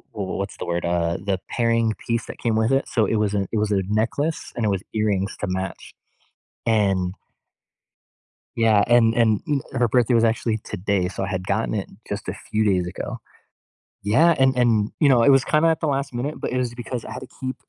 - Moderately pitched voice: No, low, 115 Hz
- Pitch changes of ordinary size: Yes, average, 3.4 semitones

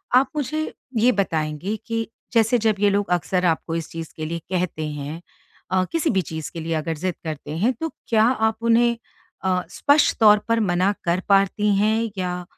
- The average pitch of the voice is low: No, high, 190 Hz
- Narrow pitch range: No, average, 5.2 semitones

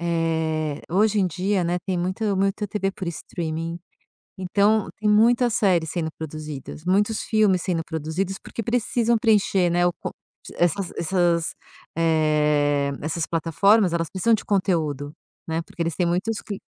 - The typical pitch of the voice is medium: Yes, medium, 175 Hz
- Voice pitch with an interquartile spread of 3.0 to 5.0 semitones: Yes, average, 3.9 semitones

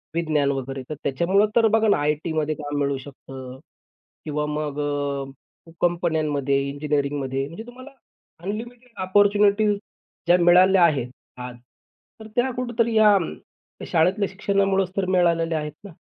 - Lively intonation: Yes, wide, 5.8 semitones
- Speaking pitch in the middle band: Yes, medium, 170 Hz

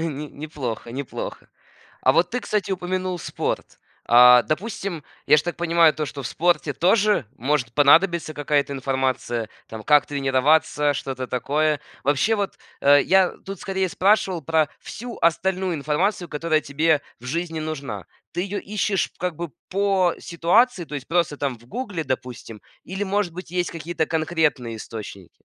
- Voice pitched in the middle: Yes, medium, 155 Hz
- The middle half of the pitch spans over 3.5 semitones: Yes, average, 4.6 semitones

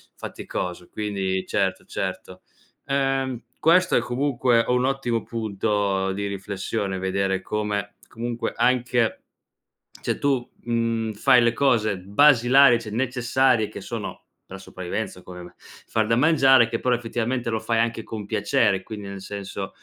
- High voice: No, low, 115 Hz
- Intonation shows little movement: No, average, 3.7 semitones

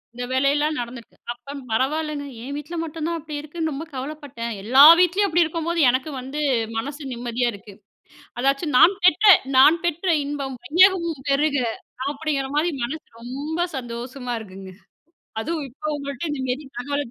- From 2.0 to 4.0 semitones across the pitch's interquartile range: Yes, average, 3.7 semitones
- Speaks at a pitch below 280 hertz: No, very high, 285 Hz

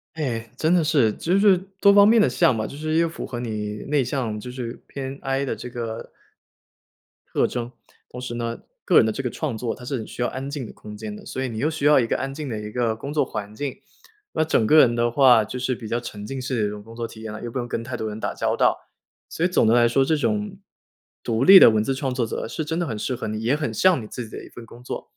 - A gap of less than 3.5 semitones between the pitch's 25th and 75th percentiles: No, average, 3.9 semitones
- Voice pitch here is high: No, low, 125 Hz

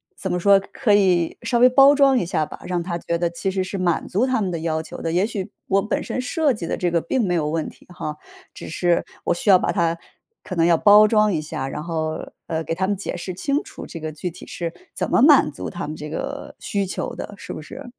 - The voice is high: No, medium, 180 Hz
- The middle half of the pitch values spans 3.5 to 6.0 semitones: Yes, average, 4.0 semitones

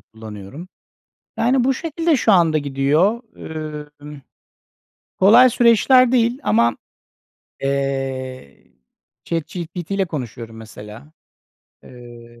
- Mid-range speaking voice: Yes, medium, 150 Hz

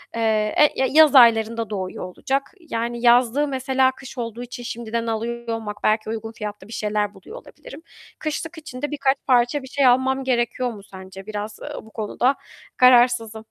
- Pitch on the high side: Yes, high, 235 Hz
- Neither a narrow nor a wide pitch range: Yes, average, 3.3 semitones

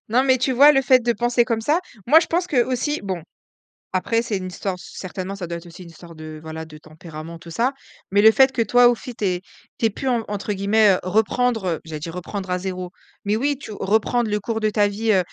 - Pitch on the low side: No, high, 210 Hz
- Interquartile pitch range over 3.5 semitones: Yes, average, 4.9 semitones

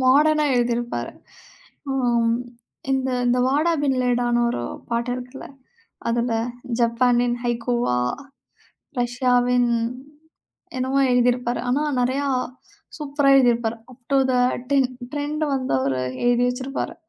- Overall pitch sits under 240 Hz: No, high, 245 Hz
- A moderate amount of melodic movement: No, narrow, 1.9 semitones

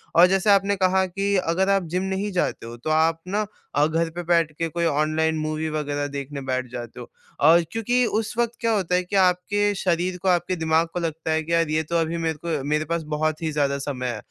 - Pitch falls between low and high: Yes, medium, 165 Hz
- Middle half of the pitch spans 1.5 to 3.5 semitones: Yes, average, 3.2 semitones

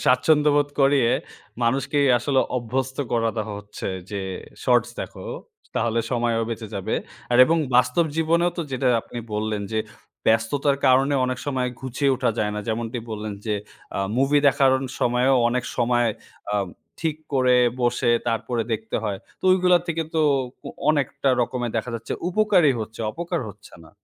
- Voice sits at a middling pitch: No, low, 125 Hz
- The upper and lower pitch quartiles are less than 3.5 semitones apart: No, average, 3.8 semitones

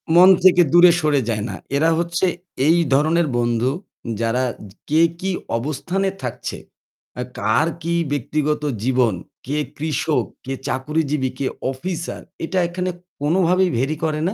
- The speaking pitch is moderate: Yes, medium, 155 Hz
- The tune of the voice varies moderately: Yes, average, 4.6 semitones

